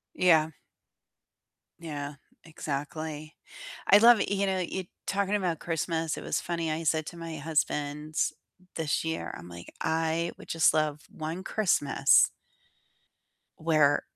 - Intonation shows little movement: Yes, narrow, 2.1 semitones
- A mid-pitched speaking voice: Yes, medium, 160 Hz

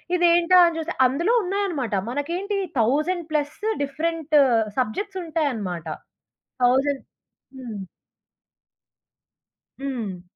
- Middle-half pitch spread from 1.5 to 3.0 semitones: No, average, 5.3 semitones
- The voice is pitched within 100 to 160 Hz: No, very high, 300 Hz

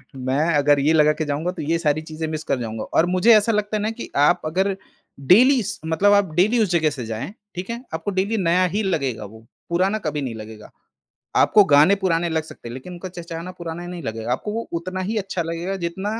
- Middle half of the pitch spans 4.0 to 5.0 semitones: Yes, average, 4.7 semitones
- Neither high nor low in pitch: Yes, medium, 170 Hz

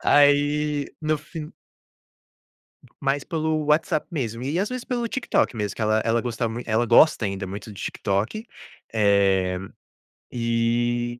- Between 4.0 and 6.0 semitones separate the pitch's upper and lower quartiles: Yes, wide, 5.6 semitones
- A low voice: Yes, low, 120 Hz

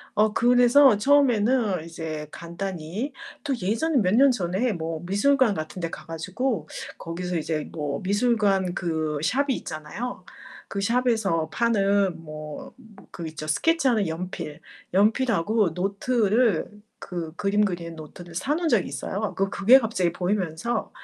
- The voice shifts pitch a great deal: Yes, wide, 6.0 semitones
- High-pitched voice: Yes, high, 195 Hz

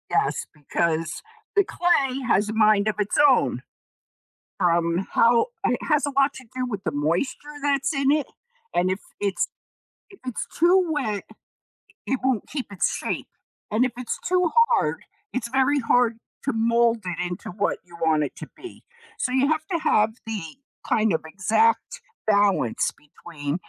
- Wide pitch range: Yes, wide, 7.0 semitones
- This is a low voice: No, high, 230 Hz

